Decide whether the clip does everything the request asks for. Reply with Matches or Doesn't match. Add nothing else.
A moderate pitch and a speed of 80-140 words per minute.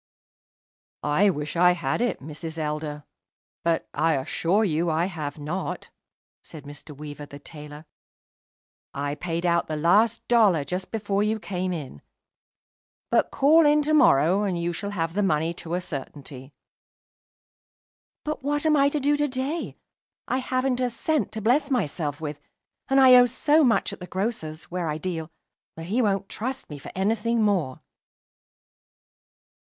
Doesn't match